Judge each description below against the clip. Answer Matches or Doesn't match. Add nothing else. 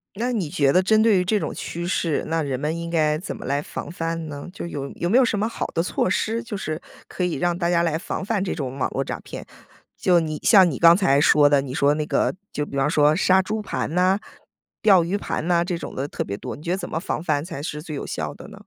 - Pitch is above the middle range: Doesn't match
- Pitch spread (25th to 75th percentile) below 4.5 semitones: Matches